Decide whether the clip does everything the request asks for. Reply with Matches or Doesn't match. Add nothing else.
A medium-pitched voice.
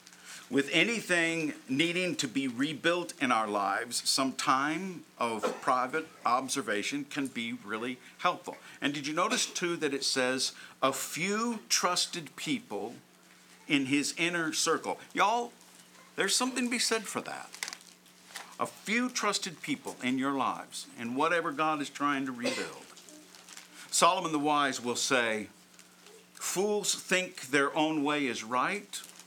Matches